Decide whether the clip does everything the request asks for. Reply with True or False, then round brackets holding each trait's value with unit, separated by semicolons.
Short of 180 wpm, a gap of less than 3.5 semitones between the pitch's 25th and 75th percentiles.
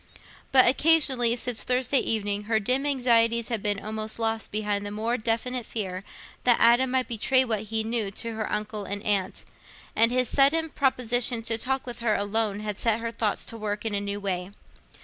False (190 wpm; 2.9 semitones)